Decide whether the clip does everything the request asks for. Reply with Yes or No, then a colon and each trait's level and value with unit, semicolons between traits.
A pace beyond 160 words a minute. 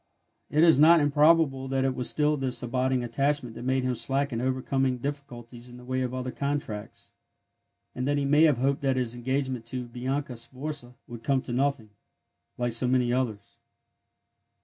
Yes: average, 180 wpm